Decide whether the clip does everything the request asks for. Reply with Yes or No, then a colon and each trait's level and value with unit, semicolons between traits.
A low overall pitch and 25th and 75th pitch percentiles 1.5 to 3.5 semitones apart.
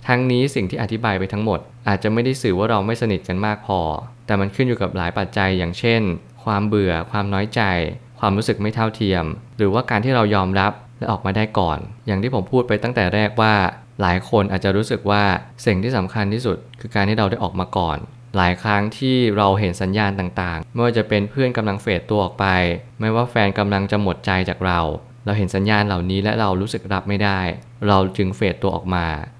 Yes: low, 100 Hz; average, 3.0 semitones